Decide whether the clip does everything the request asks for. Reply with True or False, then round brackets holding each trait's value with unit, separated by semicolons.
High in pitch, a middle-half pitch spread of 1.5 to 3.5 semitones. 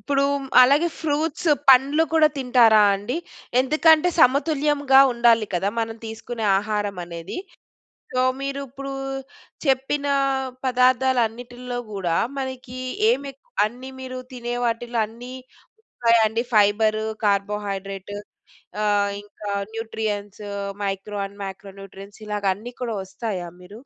False (235 Hz; 4.3 semitones)